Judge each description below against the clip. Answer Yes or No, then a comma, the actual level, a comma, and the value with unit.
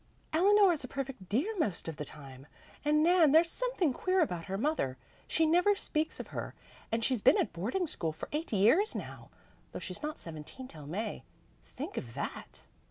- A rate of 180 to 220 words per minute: Yes, average, 190 wpm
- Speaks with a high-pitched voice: Yes, very high, 275 Hz